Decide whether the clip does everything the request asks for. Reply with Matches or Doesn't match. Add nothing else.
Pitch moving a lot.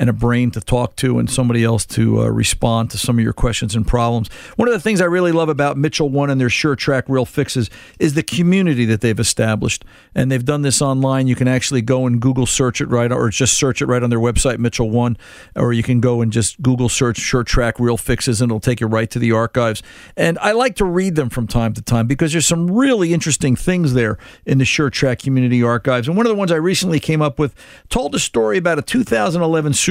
Doesn't match